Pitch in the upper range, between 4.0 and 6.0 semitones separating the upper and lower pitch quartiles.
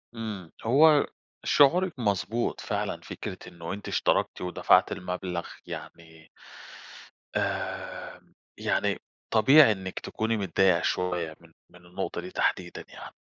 No: very low, 95 Hz; average, 4.4 semitones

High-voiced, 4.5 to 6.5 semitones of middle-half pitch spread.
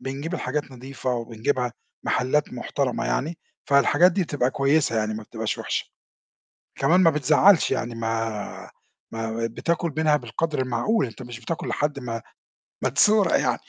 No: low, 135 Hz; average, 5.0 semitones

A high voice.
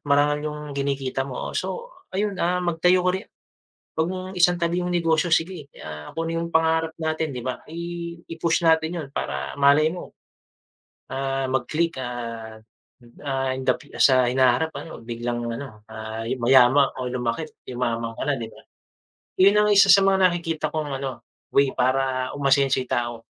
No: medium, 140 Hz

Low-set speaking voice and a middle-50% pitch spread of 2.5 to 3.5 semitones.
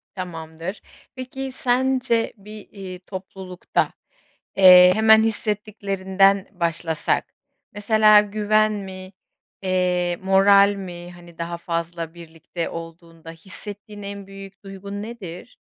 No: high, 195 Hz; average, 3.0 semitones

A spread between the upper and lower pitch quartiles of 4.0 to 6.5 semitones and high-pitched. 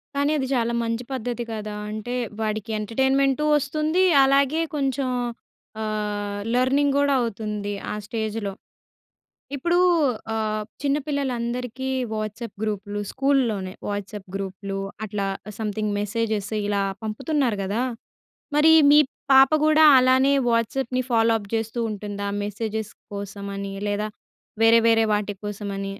Yes: average, 4.3 semitones; high, 225 Hz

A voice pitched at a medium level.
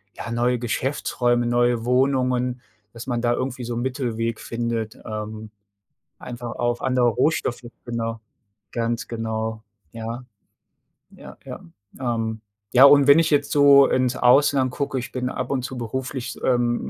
No: low, 120 Hz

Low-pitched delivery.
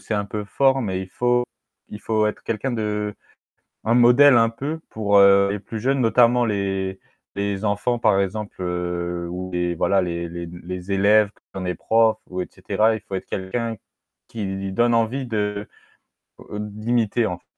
Yes: low, 105 Hz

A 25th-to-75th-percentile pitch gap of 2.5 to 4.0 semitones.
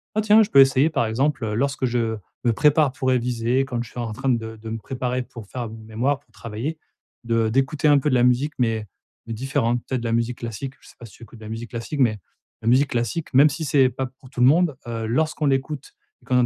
Yes: average, 3.1 semitones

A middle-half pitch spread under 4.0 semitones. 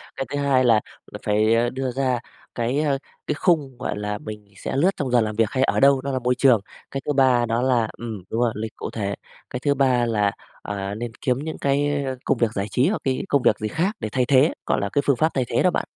Yes: average, 3.6 semitones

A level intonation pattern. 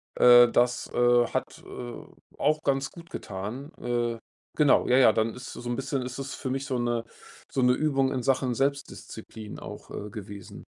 Yes: narrow, 2.3 semitones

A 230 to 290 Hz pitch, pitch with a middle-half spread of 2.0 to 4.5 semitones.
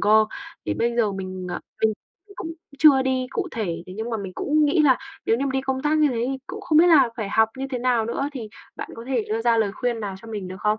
Yes: high, 235 Hz; average, 3.9 semitones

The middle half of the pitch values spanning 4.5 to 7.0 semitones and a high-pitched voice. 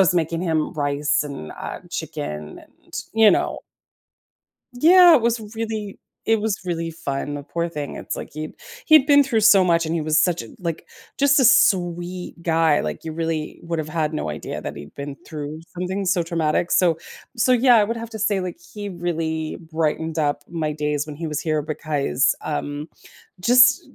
No: average, 5.2 semitones; medium, 165 Hz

